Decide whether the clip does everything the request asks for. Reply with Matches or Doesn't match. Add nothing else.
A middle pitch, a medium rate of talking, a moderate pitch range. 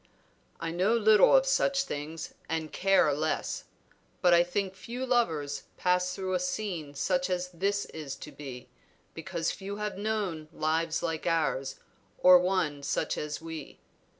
Matches